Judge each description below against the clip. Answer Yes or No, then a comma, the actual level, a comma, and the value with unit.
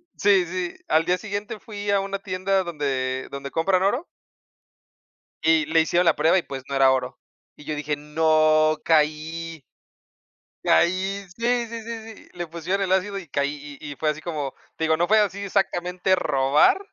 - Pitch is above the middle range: No, medium, 170 Hz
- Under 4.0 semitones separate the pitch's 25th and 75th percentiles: No, average, 4.5 semitones